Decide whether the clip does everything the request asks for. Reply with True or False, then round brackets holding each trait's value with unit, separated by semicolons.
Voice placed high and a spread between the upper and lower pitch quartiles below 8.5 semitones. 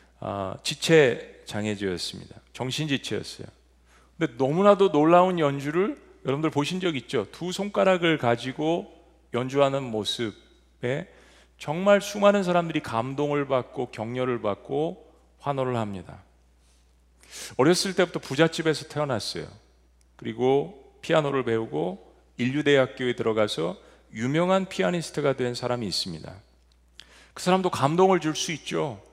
False (135 Hz; 6.8 semitones)